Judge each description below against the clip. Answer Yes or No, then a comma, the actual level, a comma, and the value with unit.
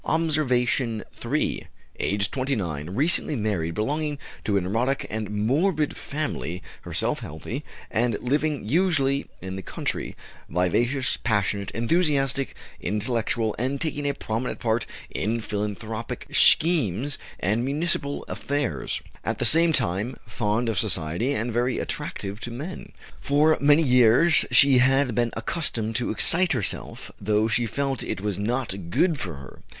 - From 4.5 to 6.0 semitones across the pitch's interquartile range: Yes, average, 5.1 semitones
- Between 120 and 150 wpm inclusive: Yes, slow, 135 wpm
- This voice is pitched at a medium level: No, low, 120 Hz